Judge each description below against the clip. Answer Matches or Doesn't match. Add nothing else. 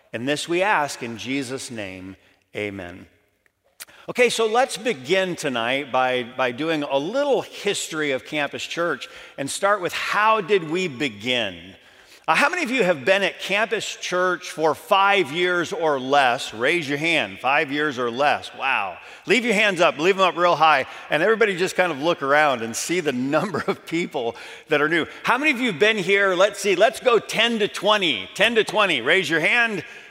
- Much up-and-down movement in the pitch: Matches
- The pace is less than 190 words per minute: Doesn't match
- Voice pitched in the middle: Matches